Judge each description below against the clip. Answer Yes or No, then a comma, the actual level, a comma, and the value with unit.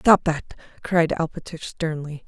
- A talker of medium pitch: Yes, medium, 160 Hz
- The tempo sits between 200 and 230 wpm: No, slow, 130 wpm